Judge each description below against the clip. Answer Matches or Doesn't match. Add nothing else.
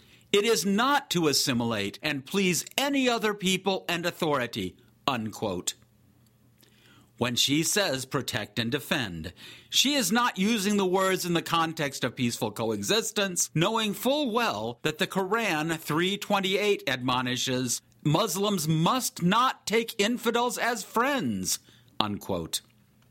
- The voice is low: Doesn't match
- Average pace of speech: Doesn't match